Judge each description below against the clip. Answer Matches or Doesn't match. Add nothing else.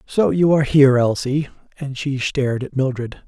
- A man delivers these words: Matches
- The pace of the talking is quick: Doesn't match